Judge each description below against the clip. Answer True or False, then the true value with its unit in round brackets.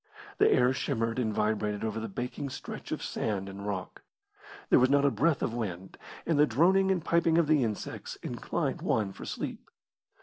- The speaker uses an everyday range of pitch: False (5.7 semitones)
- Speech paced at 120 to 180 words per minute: False (190 wpm)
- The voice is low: True (120 Hz)